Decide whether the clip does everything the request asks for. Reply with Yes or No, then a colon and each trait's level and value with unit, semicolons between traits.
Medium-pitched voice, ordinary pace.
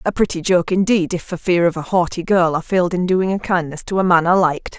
No: medium, 175 Hz; fast, 275 wpm